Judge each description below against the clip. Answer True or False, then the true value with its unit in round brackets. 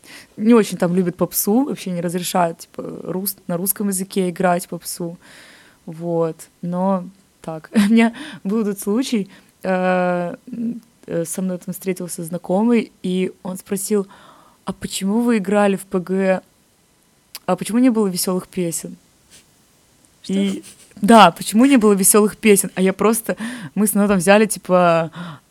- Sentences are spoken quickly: False (135 wpm)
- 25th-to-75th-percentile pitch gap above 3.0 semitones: False (2.7 semitones)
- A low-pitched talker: False (190 Hz)